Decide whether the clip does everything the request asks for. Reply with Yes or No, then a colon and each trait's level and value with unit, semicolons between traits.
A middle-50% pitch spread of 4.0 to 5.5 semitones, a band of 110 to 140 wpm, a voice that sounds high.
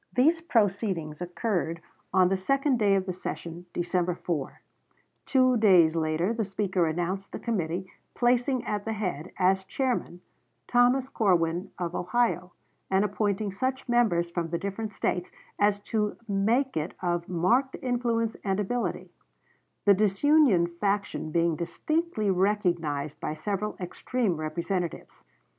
Yes: average, 4.8 semitones; slow, 135 wpm; high, 195 Hz